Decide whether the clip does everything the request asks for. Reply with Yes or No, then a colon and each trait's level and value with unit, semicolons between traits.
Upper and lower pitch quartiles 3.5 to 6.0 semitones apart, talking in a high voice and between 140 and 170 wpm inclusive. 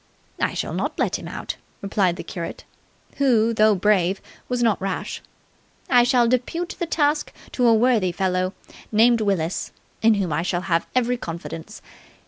Yes: average, 4.9 semitones; high, 215 Hz; average, 160 wpm